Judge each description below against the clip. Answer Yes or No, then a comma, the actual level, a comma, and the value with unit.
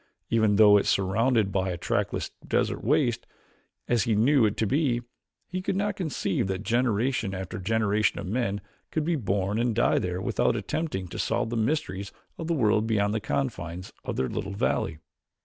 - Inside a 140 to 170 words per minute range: No, average, 185 wpm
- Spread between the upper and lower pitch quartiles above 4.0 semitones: Yes, average, 4.6 semitones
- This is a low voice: Yes, low, 110 Hz